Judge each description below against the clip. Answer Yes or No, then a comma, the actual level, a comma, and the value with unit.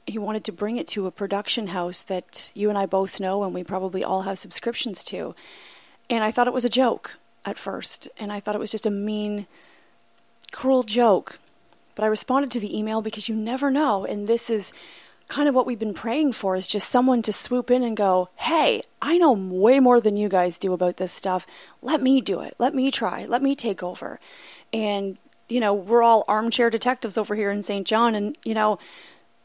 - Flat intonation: No, average, 3.5 semitones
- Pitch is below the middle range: No, high, 215 Hz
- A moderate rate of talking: No, fast, 220 wpm